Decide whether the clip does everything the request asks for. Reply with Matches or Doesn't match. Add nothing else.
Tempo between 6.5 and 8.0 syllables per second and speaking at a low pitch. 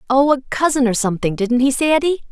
Doesn't match